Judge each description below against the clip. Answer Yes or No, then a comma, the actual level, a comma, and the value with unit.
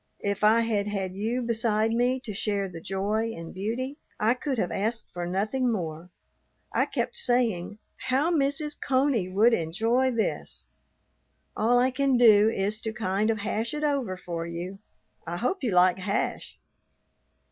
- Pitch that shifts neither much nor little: Yes, average, 4.3 semitones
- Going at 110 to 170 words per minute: Yes, average, 160 wpm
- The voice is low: No, high, 220 Hz